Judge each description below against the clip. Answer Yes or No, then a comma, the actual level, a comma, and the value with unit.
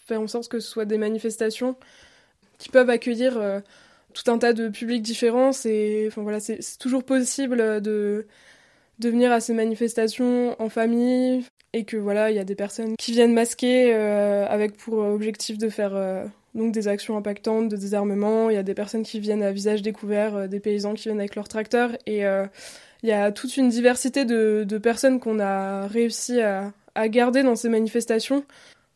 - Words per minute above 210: No, average, 195 wpm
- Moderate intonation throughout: No, narrow, 2.2 semitones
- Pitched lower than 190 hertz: No, high, 225 Hz